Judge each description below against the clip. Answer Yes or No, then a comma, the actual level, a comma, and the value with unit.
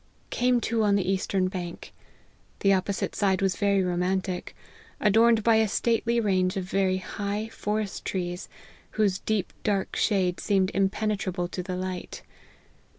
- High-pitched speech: Yes, high, 195 Hz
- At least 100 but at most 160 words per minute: Yes, average, 145 wpm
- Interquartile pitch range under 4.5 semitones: Yes, narrow, 2.4 semitones